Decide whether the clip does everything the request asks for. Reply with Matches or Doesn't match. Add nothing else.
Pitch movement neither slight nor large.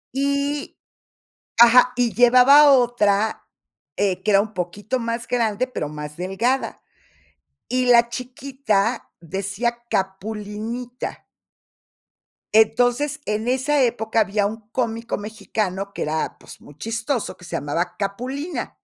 Matches